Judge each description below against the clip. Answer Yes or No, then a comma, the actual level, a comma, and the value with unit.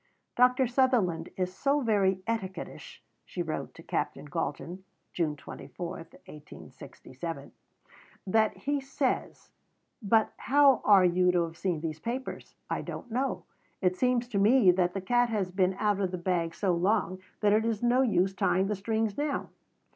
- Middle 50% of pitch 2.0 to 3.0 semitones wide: No, average, 4.9 semitones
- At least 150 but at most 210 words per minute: Yes, average, 160 wpm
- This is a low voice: No, high, 195 Hz